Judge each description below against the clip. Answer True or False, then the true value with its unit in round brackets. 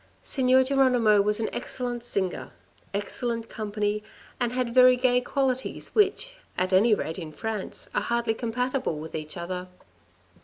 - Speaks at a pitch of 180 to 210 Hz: False (235 Hz)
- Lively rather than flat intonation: False (3.9 semitones)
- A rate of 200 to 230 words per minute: False (145 wpm)